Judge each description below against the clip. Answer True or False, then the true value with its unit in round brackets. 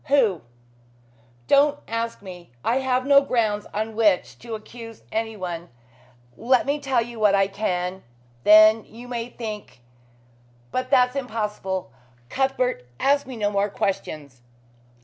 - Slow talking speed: True (130 wpm)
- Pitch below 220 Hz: False (225 Hz)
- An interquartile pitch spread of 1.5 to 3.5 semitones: False (3.9 semitones)